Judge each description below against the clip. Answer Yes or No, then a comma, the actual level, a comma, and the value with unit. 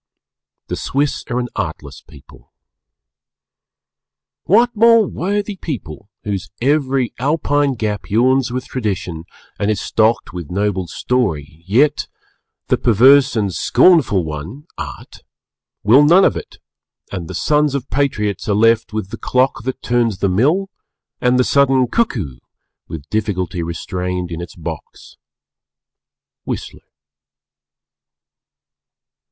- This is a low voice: Yes, low, 115 Hz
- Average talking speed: No, slow, 120 wpm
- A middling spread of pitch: No, wide, 6.7 semitones